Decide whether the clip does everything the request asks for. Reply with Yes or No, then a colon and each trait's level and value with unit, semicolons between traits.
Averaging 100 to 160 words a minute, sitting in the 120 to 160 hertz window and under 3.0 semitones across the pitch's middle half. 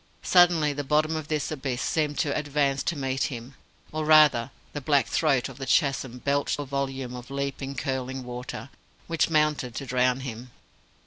No: average, 175 wpm; medium, 140 Hz; narrow, 2.5 semitones